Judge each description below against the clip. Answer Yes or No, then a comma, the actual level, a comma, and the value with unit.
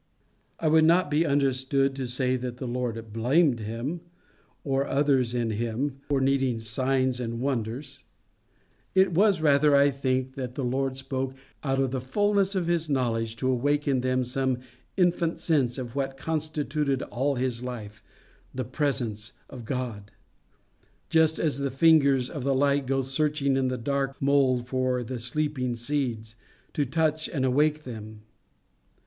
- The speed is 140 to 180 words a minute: Yes, average, 155 wpm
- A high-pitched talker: No, low, 135 Hz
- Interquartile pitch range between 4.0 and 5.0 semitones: No, average, 2.7 semitones